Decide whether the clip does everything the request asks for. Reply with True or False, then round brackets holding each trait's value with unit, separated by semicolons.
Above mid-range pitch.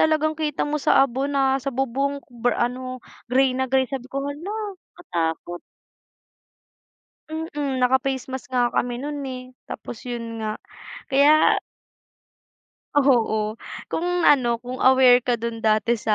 True (260 Hz)